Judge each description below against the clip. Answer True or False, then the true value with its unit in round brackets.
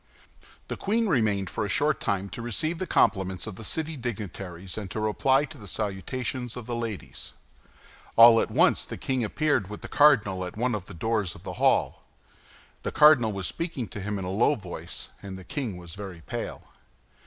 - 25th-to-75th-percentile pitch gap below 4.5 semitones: False (5.1 semitones)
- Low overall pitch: True (110 Hz)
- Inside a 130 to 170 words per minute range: False (200 wpm)